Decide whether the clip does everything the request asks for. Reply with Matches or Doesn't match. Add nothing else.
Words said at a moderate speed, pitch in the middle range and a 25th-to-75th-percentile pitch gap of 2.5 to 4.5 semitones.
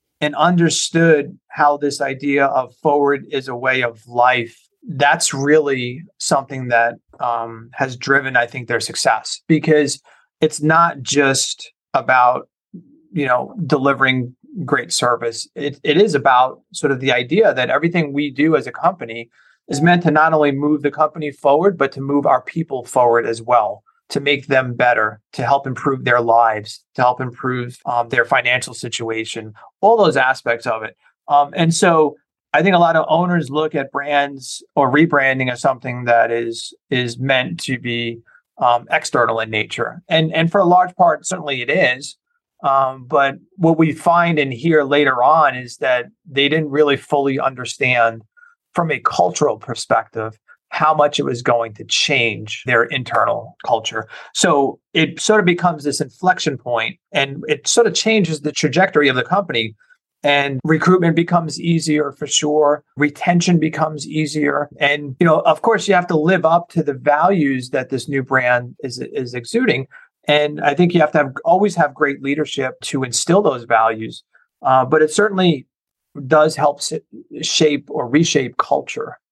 Matches